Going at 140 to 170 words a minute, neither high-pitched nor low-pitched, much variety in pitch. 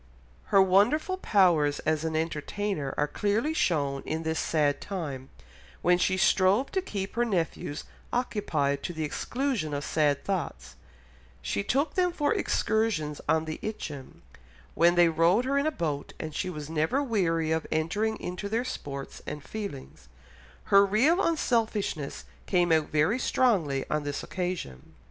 Yes: average, 155 wpm; medium, 175 Hz; wide, 6.2 semitones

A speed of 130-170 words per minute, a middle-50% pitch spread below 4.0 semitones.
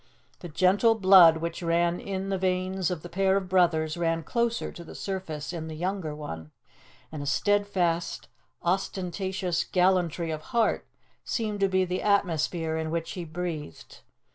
Yes: average, 160 wpm; average, 2.8 semitones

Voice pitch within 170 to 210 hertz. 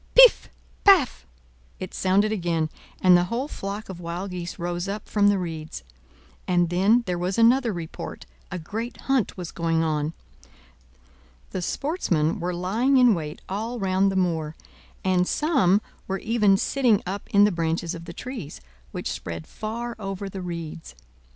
Yes: medium, 185 Hz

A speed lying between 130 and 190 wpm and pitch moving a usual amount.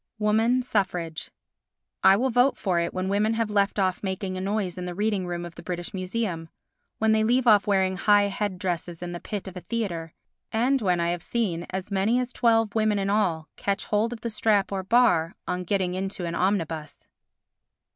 No: fast, 205 wpm; average, 3.4 semitones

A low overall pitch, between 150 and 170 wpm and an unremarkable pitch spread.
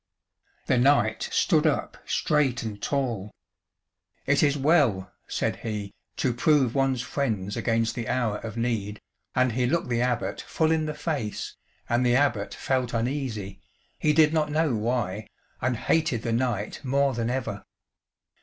Yes: low, 125 Hz; average, 155 wpm; average, 4.0 semitones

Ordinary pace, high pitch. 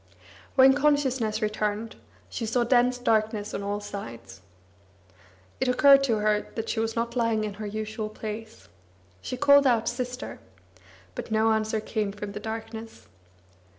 Yes: average, 150 wpm; high, 220 Hz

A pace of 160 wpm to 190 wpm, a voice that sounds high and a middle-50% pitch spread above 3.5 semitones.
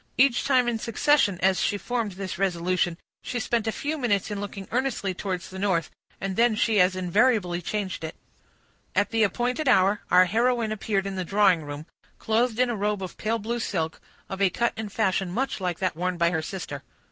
No: fast, 205 wpm; high, 200 Hz; average, 4.0 semitones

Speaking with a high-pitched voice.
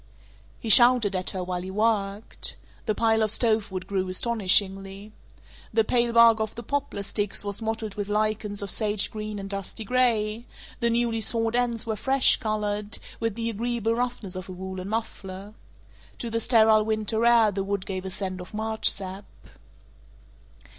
Yes: high, 215 Hz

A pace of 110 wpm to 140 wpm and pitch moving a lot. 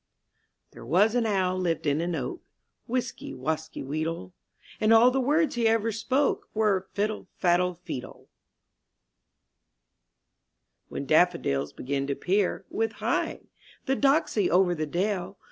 Yes: slow, 135 wpm; wide, 6.0 semitones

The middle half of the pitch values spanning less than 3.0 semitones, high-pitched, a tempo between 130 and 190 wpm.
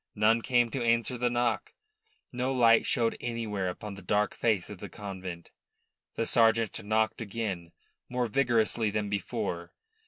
No: narrow, 2.6 semitones; low, 110 Hz; average, 150 wpm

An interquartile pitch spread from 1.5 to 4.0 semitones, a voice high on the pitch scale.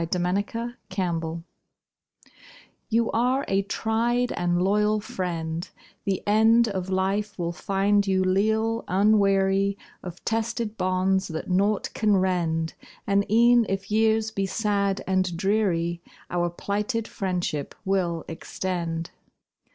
Yes: average, 3.2 semitones; high, 195 Hz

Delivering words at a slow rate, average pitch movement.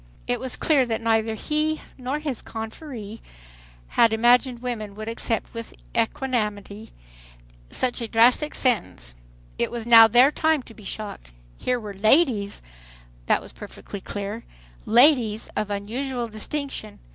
Yes: slow, 130 wpm; average, 3.3 semitones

